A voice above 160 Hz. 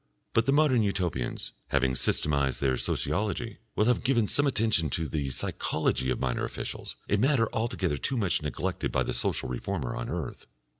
No: very low, 95 Hz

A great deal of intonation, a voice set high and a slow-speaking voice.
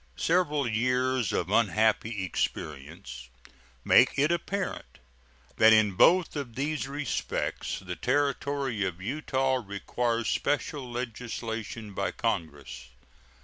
No: wide, 5.7 semitones; low, 120 Hz; slow, 105 wpm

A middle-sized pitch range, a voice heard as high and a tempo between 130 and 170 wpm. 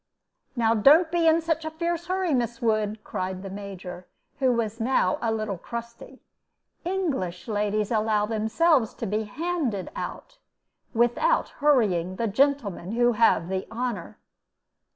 No: wide, 5.9 semitones; high, 230 Hz; average, 140 wpm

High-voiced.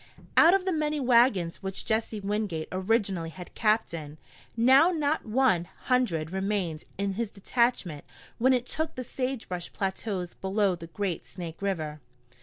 Yes: high, 205 Hz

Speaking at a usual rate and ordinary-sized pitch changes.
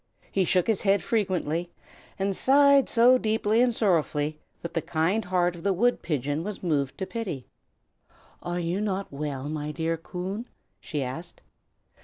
Yes: average, 160 wpm; average, 5.0 semitones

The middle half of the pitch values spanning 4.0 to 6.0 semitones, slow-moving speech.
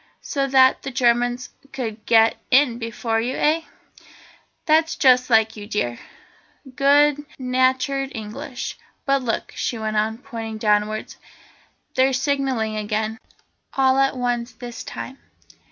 No: average, 3.3 semitones; slow, 125 wpm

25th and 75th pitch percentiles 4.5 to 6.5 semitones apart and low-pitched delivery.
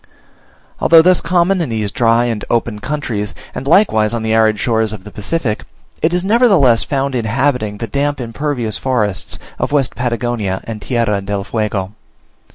Yes: average, 5.0 semitones; low, 120 Hz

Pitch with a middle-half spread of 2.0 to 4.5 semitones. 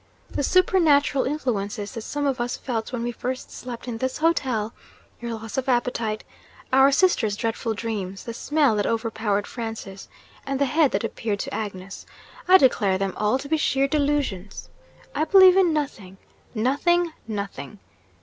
No: average, 5.0 semitones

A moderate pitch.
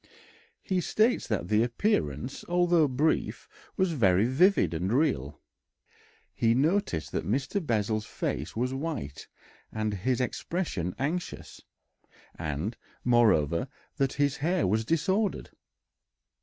No: low, 125 Hz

